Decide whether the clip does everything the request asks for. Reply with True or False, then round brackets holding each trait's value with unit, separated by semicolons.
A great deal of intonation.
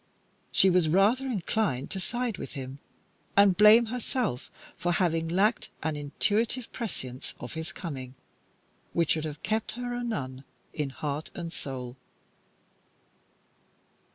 True (7.1 semitones)